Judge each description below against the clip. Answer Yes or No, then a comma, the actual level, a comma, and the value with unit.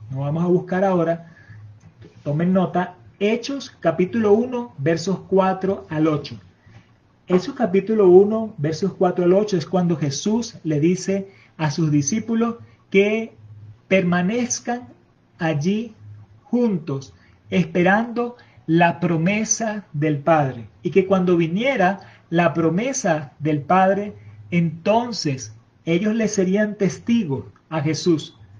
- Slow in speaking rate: Yes, slow, 110 wpm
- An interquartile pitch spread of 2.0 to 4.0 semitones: No, average, 5.2 semitones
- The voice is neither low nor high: Yes, medium, 175 Hz